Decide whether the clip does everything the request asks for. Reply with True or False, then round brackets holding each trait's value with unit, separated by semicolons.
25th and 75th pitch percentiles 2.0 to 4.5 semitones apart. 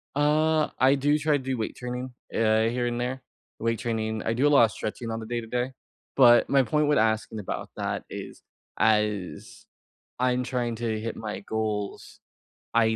True (2.9 semitones)